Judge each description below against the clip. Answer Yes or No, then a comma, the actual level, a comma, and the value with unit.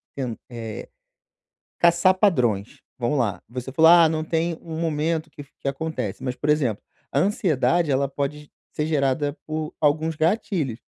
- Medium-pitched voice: Yes, medium, 150 Hz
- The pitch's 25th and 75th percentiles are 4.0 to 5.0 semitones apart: No, average, 3.6 semitones